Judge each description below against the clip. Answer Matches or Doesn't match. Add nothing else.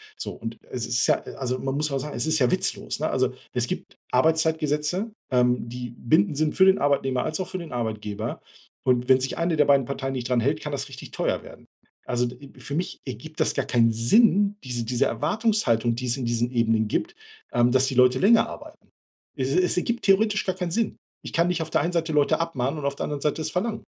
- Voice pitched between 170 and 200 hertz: Doesn't match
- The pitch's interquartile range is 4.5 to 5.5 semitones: Matches